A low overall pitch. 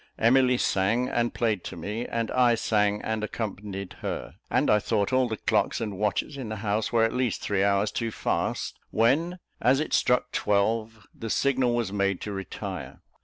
Yes: low, 110 Hz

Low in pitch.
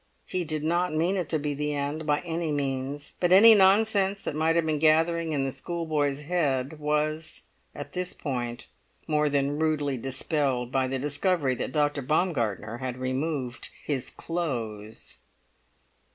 No: medium, 150 Hz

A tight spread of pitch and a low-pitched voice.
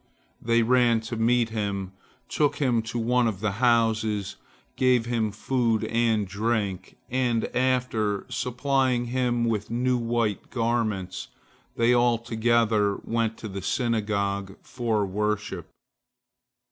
Yes: narrow, 2.3 semitones; low, 115 Hz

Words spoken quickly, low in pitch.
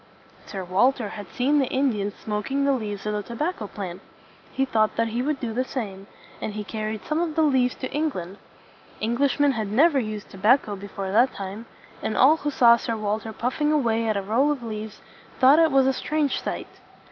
No: fast, 215 wpm; high, 230 Hz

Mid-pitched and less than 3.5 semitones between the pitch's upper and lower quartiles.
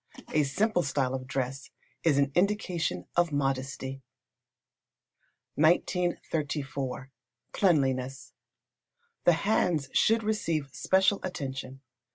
No: medium, 145 Hz; average, 4.8 semitones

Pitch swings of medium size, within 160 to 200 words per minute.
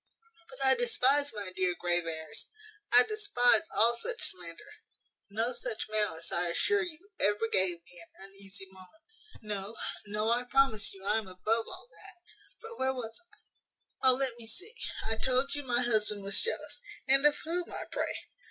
No: wide, 5.7 semitones; average, 170 wpm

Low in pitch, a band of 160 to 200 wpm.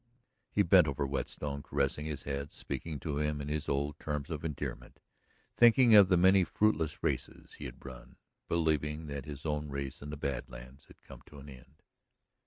Yes: very low, 75 Hz; average, 190 wpm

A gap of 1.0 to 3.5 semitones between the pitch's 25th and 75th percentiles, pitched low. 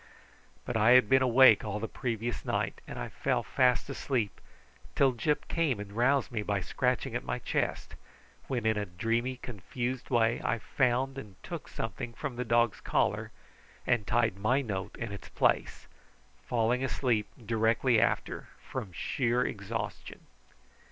Yes: average, 2.8 semitones; low, 120 Hz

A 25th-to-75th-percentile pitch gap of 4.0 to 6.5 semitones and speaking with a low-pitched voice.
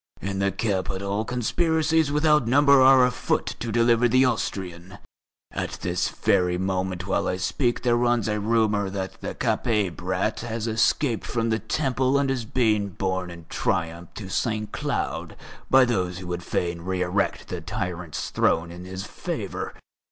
Yes: average, 4.8 semitones; low, 105 Hz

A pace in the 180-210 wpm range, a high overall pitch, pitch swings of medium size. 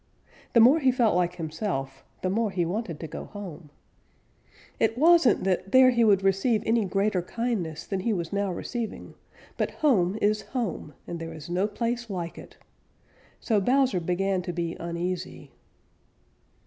No: average, 160 wpm; high, 195 Hz; average, 5.0 semitones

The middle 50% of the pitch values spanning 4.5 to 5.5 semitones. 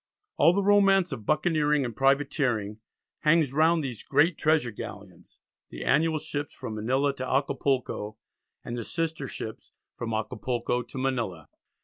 Yes: average, 5.2 semitones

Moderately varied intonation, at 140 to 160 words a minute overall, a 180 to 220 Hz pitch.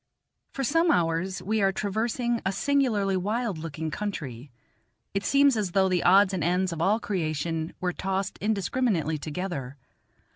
Yes: average, 4.6 semitones; average, 150 wpm; high, 190 Hz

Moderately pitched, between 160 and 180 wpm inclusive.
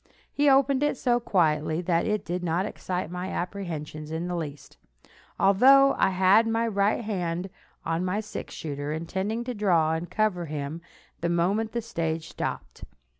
Yes: medium, 180 Hz; average, 165 wpm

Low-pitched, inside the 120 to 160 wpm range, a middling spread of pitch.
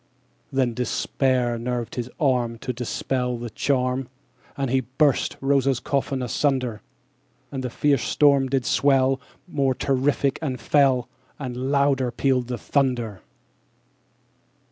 No: low, 130 Hz; slow, 135 wpm; narrow, 1.9 semitones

